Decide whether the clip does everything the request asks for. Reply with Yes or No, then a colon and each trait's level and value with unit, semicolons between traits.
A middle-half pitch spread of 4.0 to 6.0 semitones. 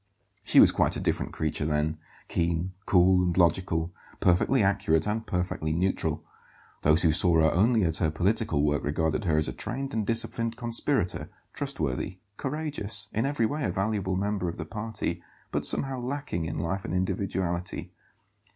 Yes: average, 5.1 semitones